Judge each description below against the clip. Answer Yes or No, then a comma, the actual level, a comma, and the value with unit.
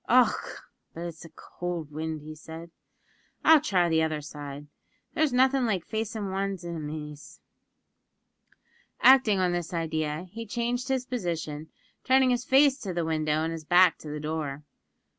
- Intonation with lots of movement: Yes, wide, 6.9 semitones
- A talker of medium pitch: Yes, medium, 175 Hz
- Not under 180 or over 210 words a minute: No, average, 155 wpm